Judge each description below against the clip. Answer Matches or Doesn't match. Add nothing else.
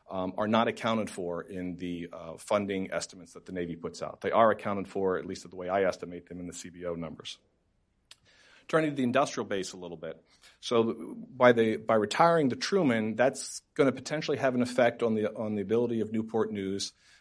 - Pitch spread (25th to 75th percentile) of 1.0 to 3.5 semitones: Doesn't match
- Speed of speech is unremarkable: Doesn't match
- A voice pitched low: Matches